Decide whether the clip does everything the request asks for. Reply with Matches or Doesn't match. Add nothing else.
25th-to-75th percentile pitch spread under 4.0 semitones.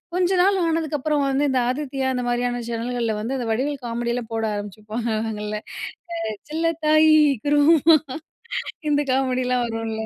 Doesn't match